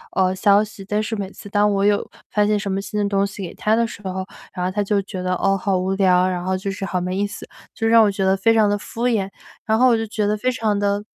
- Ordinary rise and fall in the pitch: No, narrow, 1.8 semitones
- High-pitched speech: Yes, high, 205 Hz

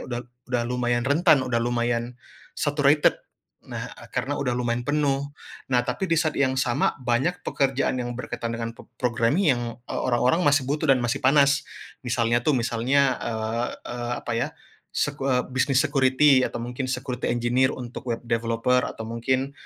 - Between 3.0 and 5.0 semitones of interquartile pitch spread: No, narrow, 2.6 semitones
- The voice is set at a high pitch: No, low, 125 Hz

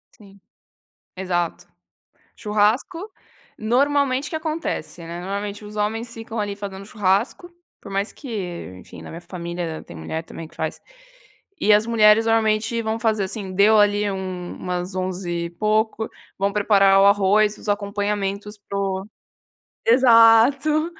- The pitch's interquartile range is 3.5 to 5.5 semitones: No, average, 2.8 semitones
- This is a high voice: Yes, high, 205 Hz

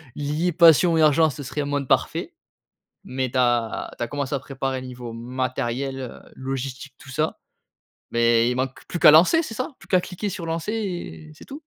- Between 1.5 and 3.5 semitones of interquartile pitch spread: No, average, 4.5 semitones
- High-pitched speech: No, low, 135 Hz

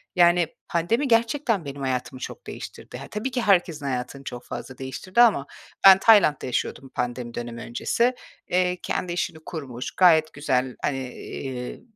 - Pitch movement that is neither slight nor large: No, wide, 6.6 semitones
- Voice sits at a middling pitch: Yes, medium, 150 Hz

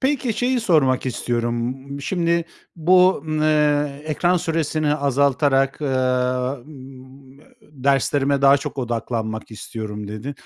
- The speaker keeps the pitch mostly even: No, average, 3.3 semitones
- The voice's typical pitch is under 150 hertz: Yes, medium, 140 Hz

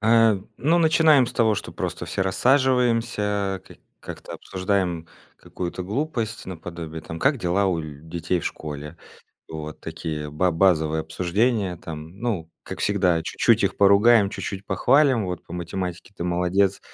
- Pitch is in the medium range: No, very low, 95 Hz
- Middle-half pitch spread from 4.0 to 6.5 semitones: Yes, average, 5.2 semitones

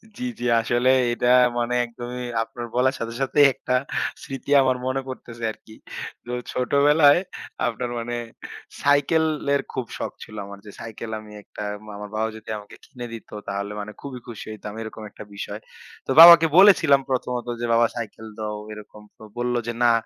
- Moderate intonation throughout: Yes, average, 3.5 semitones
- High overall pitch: No, low, 120 Hz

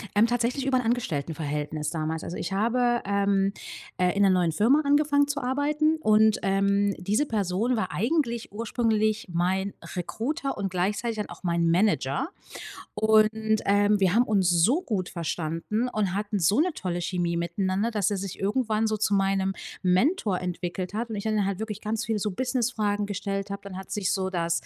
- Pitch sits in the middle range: No, high, 205 Hz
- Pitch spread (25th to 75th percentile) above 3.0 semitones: Yes, average, 3.7 semitones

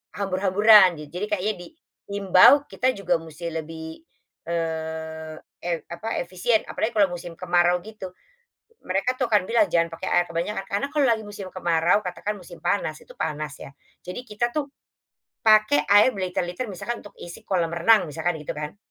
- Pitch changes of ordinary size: Yes, average, 4.0 semitones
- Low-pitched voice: No, medium, 185 Hz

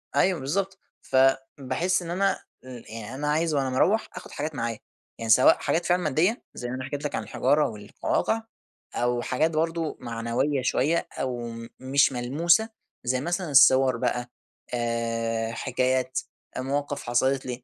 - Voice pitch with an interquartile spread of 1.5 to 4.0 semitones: No, average, 4.4 semitones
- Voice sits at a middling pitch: No, low, 130 Hz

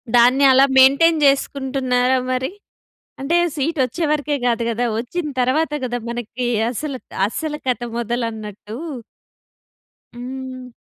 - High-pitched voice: Yes, very high, 255 Hz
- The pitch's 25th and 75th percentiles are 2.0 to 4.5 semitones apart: Yes, narrow, 2.6 semitones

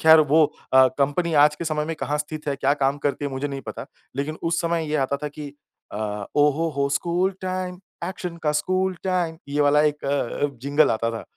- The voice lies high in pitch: No, medium, 150 Hz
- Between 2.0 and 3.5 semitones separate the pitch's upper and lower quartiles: Yes, average, 2.8 semitones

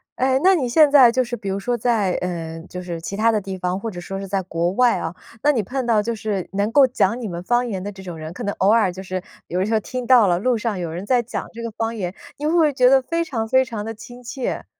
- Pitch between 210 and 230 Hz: Yes, high, 220 Hz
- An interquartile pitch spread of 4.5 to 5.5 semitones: Yes, average, 4.8 semitones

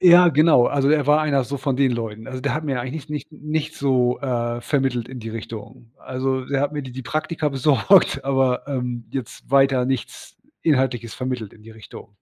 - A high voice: No, low, 130 Hz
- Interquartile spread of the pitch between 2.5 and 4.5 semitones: Yes, average, 2.8 semitones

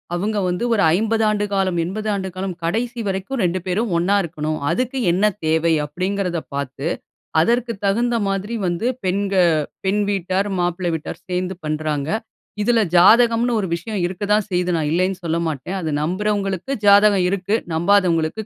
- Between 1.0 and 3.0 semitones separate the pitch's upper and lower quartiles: No, average, 3.5 semitones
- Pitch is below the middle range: No, high, 190 Hz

